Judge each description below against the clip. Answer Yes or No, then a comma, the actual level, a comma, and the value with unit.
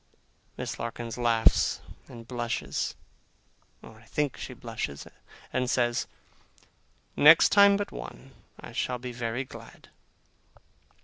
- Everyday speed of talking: No, slow, 115 wpm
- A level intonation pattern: Yes, narrow, 1.9 semitones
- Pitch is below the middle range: Yes, low, 120 Hz